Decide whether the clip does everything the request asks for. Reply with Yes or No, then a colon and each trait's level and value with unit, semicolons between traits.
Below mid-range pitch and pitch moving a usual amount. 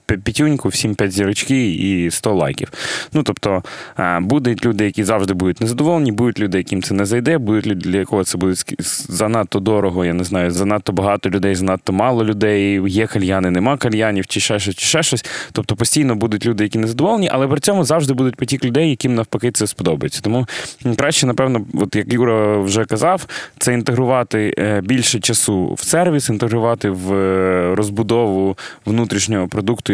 Yes: low, 110 Hz; average, 3.7 semitones